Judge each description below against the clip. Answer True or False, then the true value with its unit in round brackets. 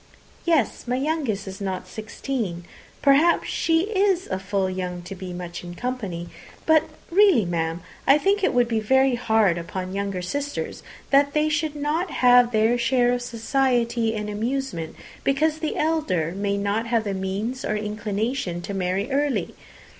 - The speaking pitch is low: False (230 Hz)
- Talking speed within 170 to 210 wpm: False (160 wpm)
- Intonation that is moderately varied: False (6.4 semitones)